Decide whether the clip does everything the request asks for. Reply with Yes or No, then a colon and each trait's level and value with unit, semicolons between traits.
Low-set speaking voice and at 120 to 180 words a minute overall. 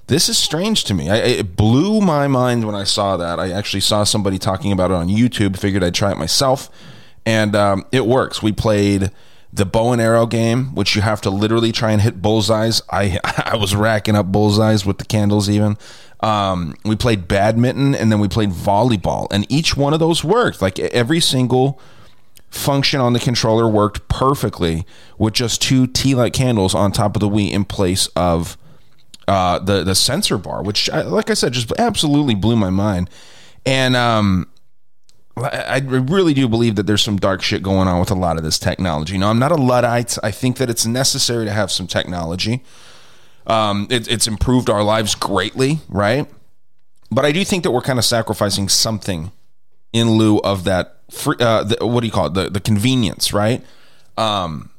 No: low, 110 Hz; average, 195 wpm